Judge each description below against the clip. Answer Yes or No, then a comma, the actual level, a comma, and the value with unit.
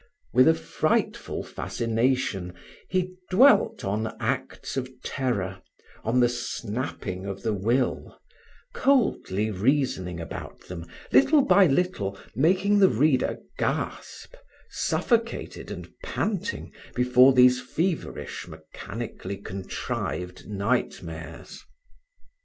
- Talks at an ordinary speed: No, slow, 95 wpm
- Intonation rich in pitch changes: Yes, wide, 8.4 semitones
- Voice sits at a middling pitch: No, low, 125 Hz